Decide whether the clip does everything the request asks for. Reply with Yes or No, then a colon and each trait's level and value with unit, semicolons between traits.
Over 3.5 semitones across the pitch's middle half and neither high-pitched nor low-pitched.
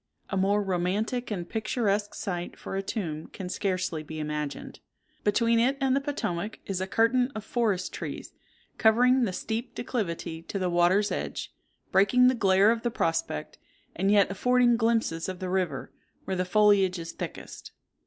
No: average, 4.1 semitones; high, 200 Hz